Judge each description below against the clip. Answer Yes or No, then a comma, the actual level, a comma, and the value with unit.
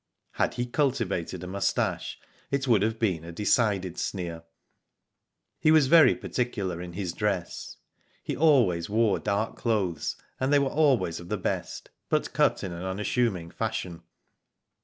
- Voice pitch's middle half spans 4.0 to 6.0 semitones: Yes, wide, 5.6 semitones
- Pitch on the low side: Yes, low, 105 Hz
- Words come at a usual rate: Yes, average, 155 wpm